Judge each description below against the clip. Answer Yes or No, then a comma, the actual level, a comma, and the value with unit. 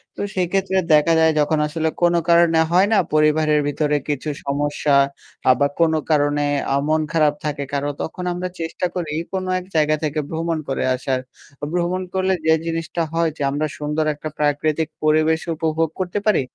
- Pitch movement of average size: No, narrow, 2.2 semitones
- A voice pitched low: No, medium, 155 Hz